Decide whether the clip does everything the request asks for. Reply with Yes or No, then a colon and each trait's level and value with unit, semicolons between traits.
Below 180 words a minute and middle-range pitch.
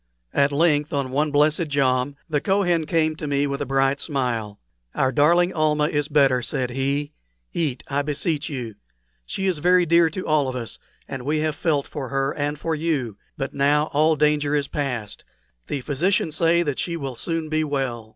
No: average, 195 wpm; medium, 145 Hz